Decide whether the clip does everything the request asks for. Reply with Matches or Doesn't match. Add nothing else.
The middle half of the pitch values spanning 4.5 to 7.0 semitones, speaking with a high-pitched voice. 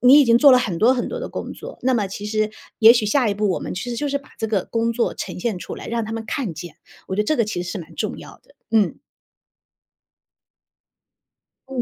Doesn't match